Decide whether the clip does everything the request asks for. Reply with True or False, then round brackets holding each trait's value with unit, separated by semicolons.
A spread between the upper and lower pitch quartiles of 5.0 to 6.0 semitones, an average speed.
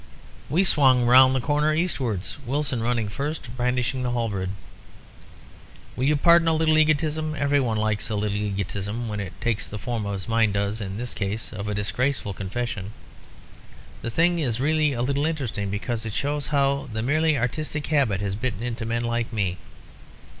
True (5.3 semitones; 175 wpm)